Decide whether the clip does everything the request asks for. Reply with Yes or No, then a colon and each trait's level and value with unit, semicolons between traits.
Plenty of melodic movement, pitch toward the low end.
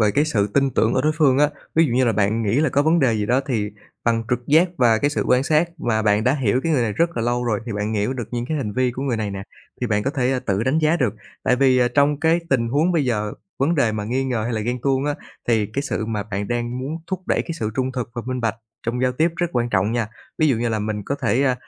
No: average, 4.1 semitones; low, 125 Hz